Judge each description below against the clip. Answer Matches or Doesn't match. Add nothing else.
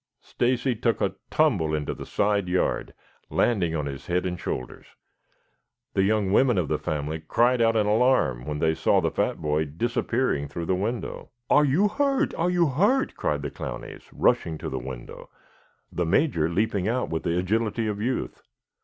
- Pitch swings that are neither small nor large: Doesn't match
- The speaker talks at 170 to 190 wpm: Matches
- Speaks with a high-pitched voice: Doesn't match